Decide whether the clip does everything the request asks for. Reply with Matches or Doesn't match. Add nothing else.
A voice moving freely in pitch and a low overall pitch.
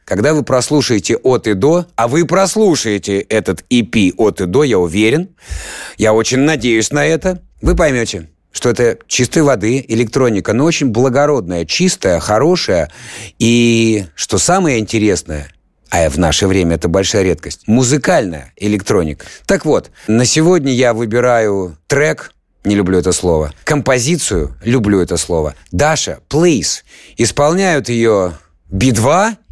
Matches